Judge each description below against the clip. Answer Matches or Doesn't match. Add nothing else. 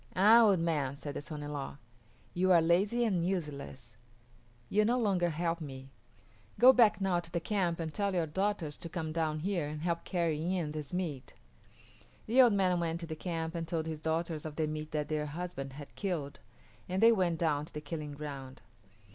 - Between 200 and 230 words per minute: Matches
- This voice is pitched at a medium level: Matches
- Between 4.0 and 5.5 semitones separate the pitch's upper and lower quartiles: Doesn't match